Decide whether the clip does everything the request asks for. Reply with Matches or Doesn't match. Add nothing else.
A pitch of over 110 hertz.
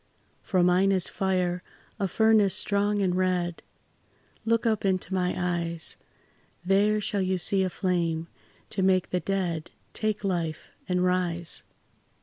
Matches